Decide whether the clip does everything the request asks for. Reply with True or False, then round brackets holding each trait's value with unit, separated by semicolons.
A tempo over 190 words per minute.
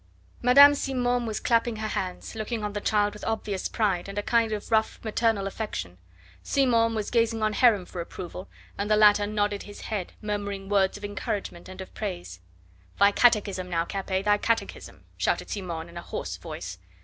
False (185 wpm)